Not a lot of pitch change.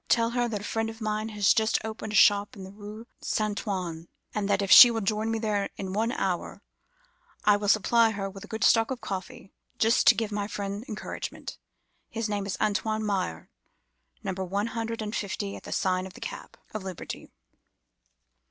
Yes: narrow, 2.0 semitones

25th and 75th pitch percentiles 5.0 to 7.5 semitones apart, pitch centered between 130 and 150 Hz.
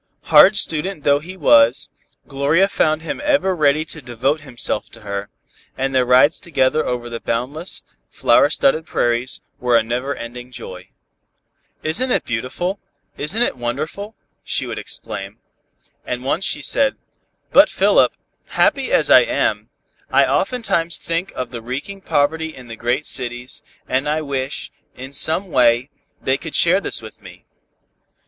Yes: average, 5.3 semitones; medium, 140 Hz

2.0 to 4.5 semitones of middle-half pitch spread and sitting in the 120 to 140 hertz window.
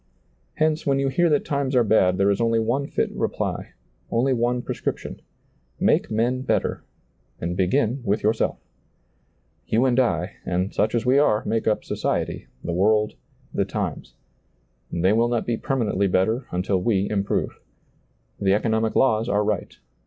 No: average, 4.0 semitones; low, 110 Hz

